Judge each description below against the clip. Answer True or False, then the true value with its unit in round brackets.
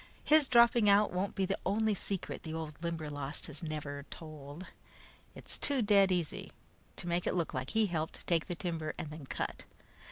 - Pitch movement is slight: False (4.4 semitones)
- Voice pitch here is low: False (170 Hz)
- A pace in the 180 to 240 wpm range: True (185 wpm)